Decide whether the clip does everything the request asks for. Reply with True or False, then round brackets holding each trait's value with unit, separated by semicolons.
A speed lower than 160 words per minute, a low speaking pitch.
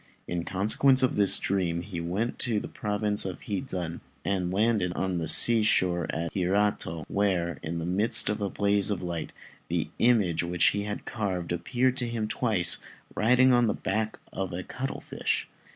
False (175 wpm; 100 Hz)